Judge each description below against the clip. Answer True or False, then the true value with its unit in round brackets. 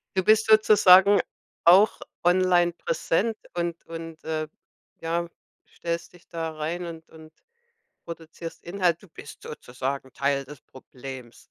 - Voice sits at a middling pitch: True (165 Hz)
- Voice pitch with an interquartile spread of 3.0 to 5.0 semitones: False (2.4 semitones)